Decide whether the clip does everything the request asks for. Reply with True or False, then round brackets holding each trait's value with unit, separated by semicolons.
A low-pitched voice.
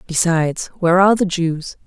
False (175 Hz)